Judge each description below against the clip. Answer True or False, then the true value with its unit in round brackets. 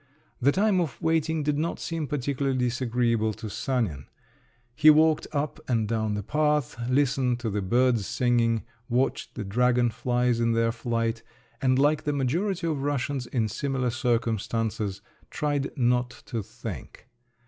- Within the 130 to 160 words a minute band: True (145 wpm)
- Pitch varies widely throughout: False (3.8 semitones)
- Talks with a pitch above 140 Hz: False (125 Hz)